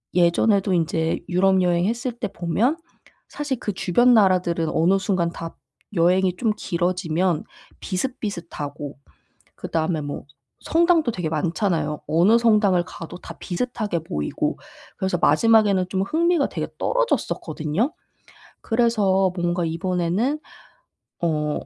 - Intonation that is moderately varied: Yes, average, 4.8 semitones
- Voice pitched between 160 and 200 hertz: Yes, medium, 185 Hz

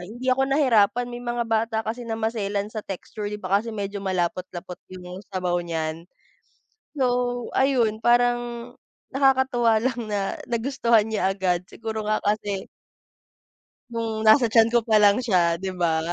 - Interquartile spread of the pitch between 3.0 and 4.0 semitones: Yes, average, 3.7 semitones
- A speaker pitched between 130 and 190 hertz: No, high, 220 Hz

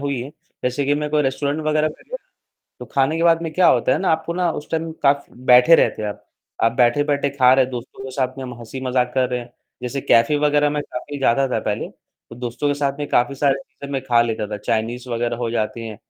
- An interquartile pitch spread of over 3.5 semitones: No, average, 3.1 semitones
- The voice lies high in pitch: No, low, 135 Hz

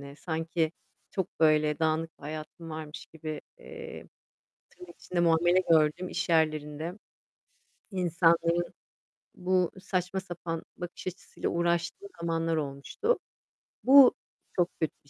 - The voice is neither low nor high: Yes, medium, 165 Hz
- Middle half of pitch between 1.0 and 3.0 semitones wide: Yes, narrow, 2.4 semitones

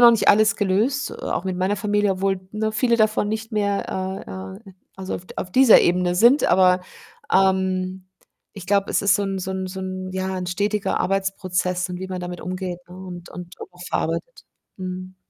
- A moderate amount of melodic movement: No, narrow, 2.0 semitones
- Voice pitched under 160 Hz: No, high, 190 Hz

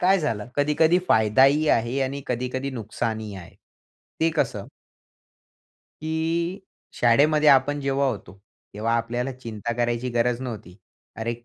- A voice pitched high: No, low, 125 Hz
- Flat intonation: No, average, 4.0 semitones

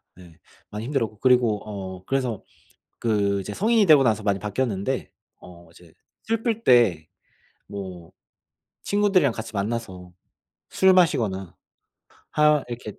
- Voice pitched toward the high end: No, low, 110 Hz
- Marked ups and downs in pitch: Yes, wide, 6.0 semitones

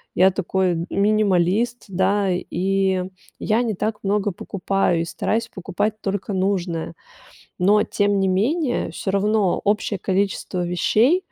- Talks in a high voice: Yes, high, 195 Hz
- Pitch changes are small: Yes, narrow, 2.3 semitones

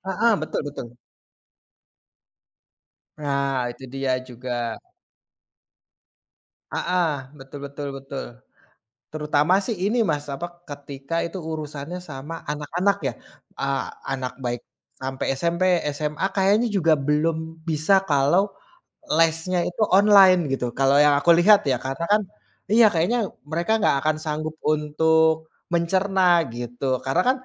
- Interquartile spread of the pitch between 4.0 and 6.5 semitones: Yes, average, 4.6 semitones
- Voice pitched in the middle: Yes, medium, 155 Hz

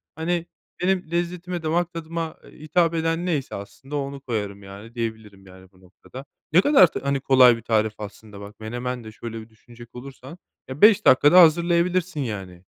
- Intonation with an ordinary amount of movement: No, wide, 7.3 semitones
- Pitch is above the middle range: No, low, 135 Hz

